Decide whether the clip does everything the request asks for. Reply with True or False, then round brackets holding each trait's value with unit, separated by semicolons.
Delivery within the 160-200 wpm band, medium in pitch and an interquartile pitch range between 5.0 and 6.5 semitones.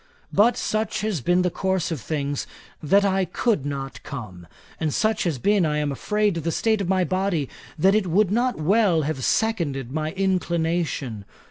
True (175 wpm; 175 Hz; 5.3 semitones)